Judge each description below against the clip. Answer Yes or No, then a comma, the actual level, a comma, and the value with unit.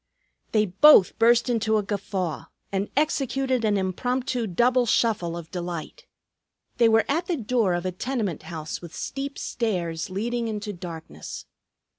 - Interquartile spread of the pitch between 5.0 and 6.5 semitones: Yes, wide, 5.4 semitones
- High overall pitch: Yes, high, 215 Hz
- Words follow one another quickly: No, average, 145 wpm